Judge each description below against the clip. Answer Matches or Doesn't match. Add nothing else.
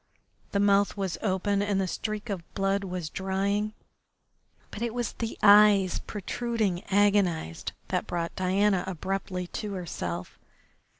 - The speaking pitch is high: Matches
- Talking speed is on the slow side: Matches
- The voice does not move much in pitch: Matches